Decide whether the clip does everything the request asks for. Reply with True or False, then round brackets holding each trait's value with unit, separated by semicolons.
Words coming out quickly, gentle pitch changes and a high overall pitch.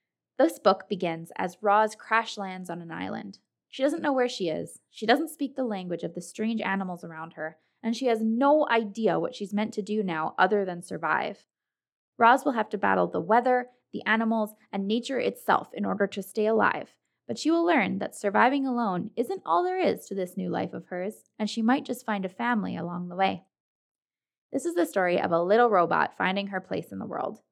False (215 wpm; 4.5 semitones; 215 Hz)